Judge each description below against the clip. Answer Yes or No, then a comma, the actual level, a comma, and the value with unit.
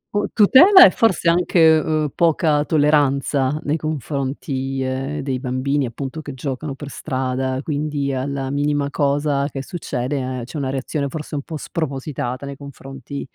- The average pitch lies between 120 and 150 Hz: Yes, medium, 140 Hz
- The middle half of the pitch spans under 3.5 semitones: Yes, narrow, 2.4 semitones